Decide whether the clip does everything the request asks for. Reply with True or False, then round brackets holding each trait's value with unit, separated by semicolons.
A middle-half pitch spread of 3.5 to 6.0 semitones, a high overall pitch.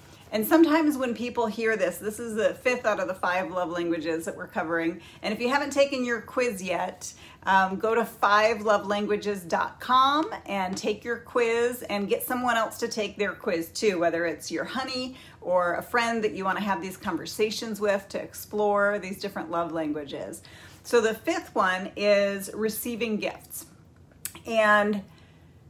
True (4.0 semitones; 210 Hz)